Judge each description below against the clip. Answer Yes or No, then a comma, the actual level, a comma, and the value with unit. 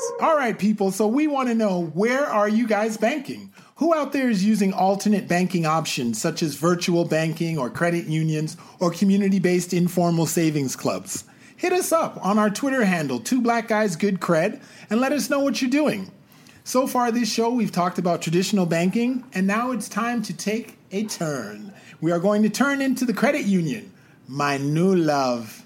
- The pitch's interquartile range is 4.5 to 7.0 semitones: Yes, wide, 5.4 semitones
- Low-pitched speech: No, high, 200 Hz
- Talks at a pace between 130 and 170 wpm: No, average, 190 wpm